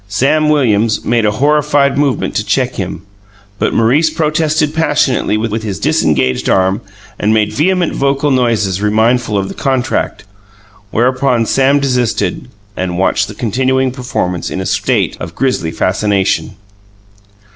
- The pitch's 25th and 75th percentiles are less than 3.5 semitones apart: No, average, 5.1 semitones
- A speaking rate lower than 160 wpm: Yes, slow, 135 wpm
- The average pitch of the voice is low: Yes, low, 120 Hz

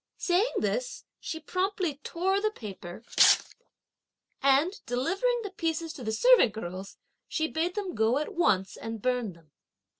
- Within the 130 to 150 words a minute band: Yes, average, 145 wpm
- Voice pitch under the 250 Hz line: No, very high, 315 Hz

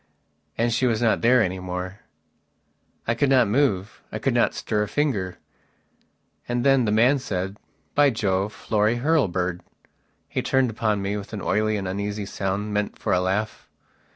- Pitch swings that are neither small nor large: Yes, average, 3.7 semitones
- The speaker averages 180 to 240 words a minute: No, average, 170 wpm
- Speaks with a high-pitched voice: No, low, 105 Hz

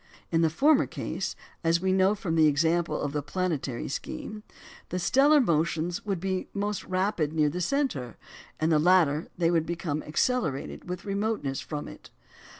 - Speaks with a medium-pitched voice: Yes, medium, 170 Hz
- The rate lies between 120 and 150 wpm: No, average, 165 wpm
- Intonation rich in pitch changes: No, average, 4.1 semitones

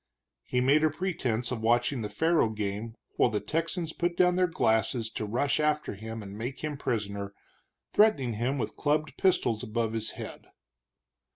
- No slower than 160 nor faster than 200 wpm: Yes, average, 170 wpm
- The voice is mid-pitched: No, low, 125 Hz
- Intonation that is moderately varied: No, wide, 5.7 semitones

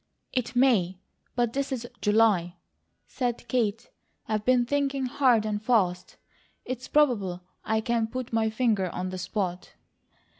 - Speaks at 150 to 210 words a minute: No, average, 140 wpm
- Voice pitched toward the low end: No, high, 225 Hz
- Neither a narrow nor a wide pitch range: Yes, average, 3.6 semitones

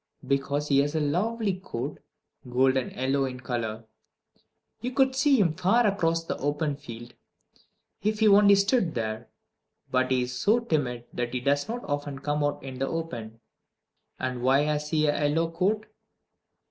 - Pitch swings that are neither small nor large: No, wide, 6.4 semitones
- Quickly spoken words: No, average, 165 wpm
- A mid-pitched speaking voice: Yes, medium, 145 Hz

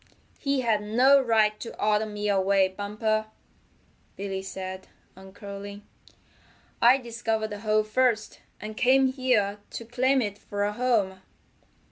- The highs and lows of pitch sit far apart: No, average, 2.9 semitones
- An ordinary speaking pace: No, slow, 130 wpm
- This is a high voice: Yes, high, 215 Hz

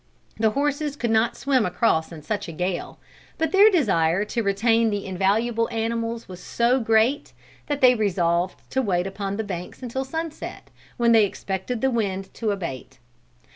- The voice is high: Yes, high, 220 Hz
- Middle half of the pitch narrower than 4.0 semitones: No, average, 4.3 semitones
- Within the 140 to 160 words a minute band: No, average, 170 wpm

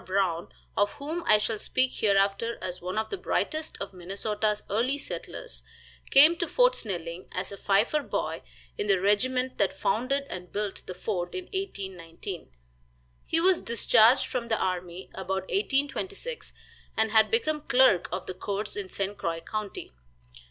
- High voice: Yes, high, 210 Hz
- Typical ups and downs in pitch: No, wide, 6.0 semitones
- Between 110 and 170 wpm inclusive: Yes, average, 160 wpm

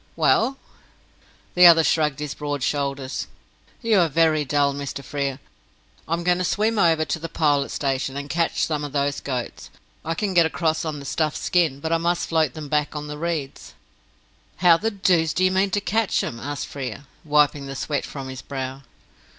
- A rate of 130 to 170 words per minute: No, average, 195 wpm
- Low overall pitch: No, medium, 150 Hz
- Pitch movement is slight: No, average, 3.2 semitones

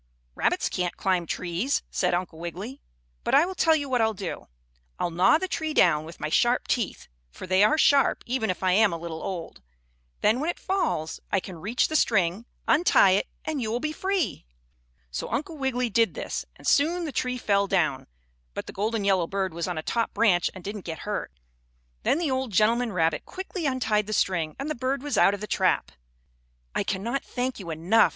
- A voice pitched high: Yes, high, 215 Hz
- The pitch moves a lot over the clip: Yes, wide, 6.7 semitones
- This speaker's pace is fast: Yes, fast, 210 wpm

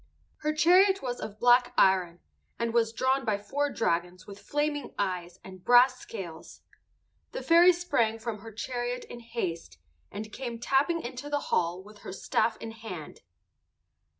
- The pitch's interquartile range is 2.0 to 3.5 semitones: No, average, 5.3 semitones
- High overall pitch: Yes, high, 230 Hz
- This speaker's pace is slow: No, average, 160 wpm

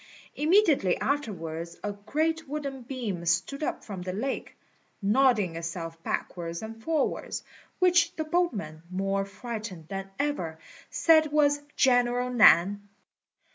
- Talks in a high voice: Yes, high, 225 Hz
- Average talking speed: No, slow, 120 wpm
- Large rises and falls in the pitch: Yes, wide, 7.9 semitones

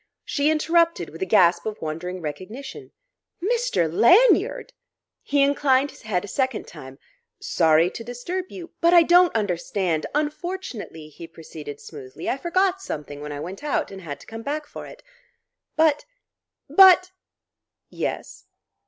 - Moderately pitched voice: No, high, 245 Hz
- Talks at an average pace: Yes, average, 155 wpm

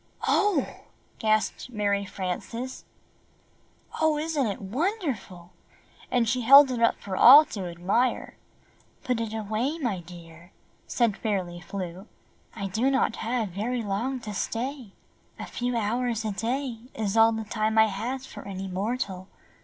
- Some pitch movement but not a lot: Yes, average, 4.3 semitones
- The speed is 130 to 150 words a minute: Yes, average, 145 wpm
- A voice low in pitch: No, high, 220 Hz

